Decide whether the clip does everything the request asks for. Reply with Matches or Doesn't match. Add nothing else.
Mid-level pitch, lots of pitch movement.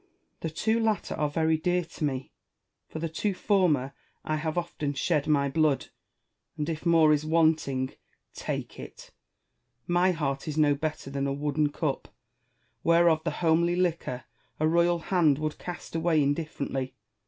Doesn't match